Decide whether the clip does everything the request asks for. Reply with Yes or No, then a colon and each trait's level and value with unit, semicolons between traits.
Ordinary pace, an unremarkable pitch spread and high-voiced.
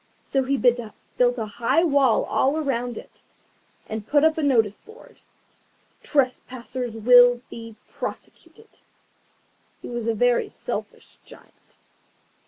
No: slow, 120 wpm; average, 3.2 semitones; high, 245 Hz